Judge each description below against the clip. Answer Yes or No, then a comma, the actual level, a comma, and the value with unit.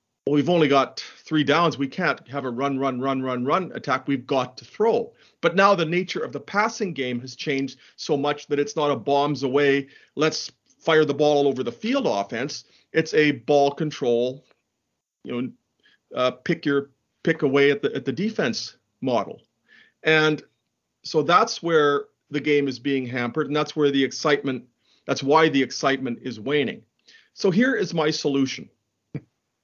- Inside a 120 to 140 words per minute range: No, average, 180 wpm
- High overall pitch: No, medium, 140 Hz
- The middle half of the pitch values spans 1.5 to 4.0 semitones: Yes, average, 2.8 semitones